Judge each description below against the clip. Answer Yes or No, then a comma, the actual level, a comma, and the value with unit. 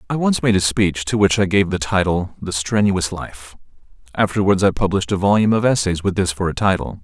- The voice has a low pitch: Yes, very low, 95 Hz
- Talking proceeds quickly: Yes, fast, 220 wpm